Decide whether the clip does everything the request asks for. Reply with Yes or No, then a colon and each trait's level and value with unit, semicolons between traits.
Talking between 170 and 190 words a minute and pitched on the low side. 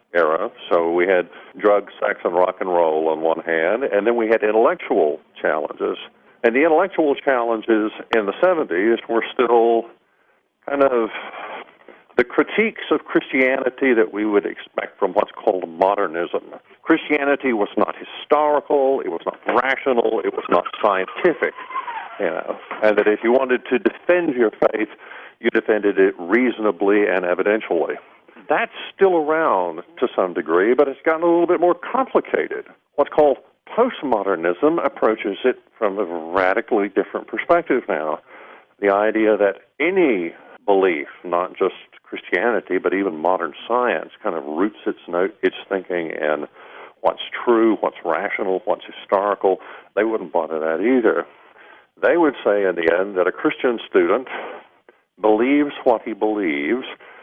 No: average, 150 wpm; low, 115 Hz